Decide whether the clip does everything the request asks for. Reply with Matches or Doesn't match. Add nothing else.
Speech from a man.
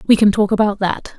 Doesn't match